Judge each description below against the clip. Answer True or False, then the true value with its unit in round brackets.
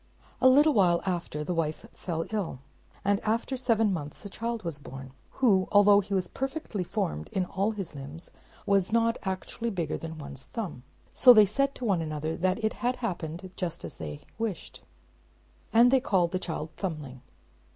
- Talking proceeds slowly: False (180 wpm)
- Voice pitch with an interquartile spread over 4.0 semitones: True (5.6 semitones)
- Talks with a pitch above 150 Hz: True (190 Hz)